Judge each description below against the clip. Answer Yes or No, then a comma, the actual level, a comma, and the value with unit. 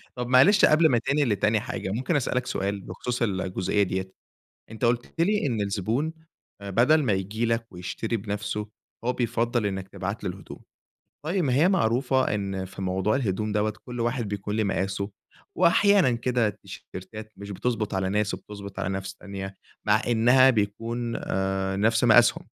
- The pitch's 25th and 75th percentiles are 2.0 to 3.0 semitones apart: No, average, 3.8 semitones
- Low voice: Yes, low, 110 Hz